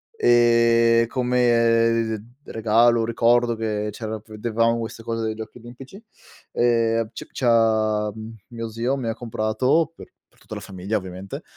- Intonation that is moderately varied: No, narrow, 1.4 semitones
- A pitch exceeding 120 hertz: No, low, 115 Hz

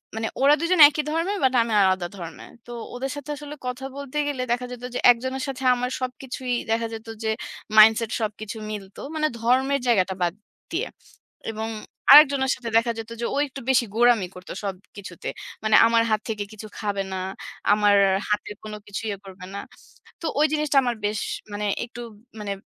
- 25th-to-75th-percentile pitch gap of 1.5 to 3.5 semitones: No, average, 4.1 semitones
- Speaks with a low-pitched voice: No, high, 230 Hz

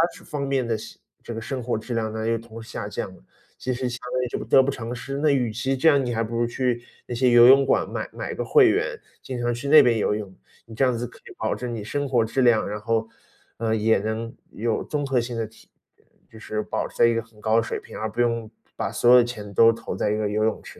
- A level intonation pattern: Yes, narrow, 2.1 semitones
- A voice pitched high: No, low, 115 Hz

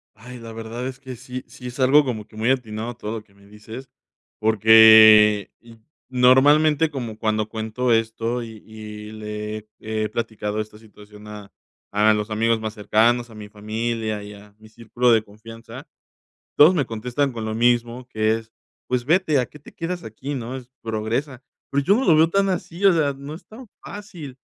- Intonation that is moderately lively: Yes, average, 3.3 semitones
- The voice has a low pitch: Yes, low, 115 Hz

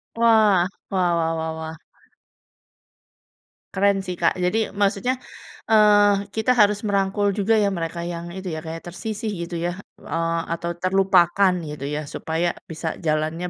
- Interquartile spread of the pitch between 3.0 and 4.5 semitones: Yes, average, 3.5 semitones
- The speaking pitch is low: No, medium, 185 Hz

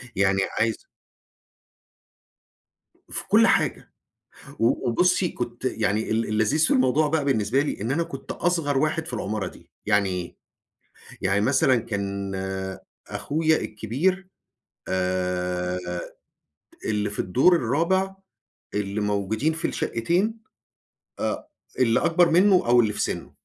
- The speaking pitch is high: No, low, 115 Hz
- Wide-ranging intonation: Yes, wide, 7.6 semitones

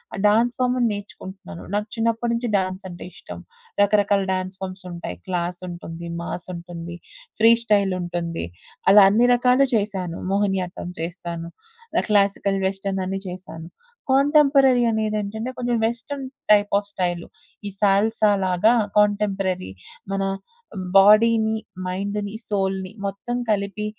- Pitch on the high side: Yes, high, 200 Hz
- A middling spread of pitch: Yes, average, 3.0 semitones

